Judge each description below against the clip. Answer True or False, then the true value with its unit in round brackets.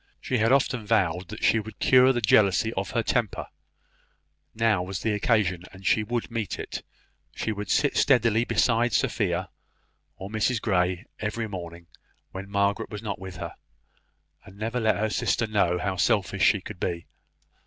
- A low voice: True (105 Hz)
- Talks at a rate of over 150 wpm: True (170 wpm)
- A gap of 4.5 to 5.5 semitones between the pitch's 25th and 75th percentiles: False (3.2 semitones)